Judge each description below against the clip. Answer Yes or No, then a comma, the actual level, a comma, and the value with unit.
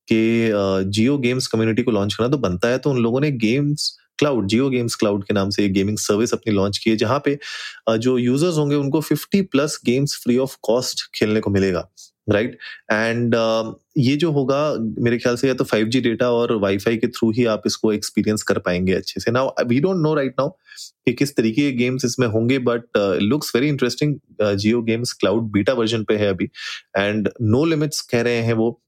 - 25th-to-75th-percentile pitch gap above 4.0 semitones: No, average, 3.5 semitones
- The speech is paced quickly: Yes, fast, 210 wpm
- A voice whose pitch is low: Yes, low, 120 Hz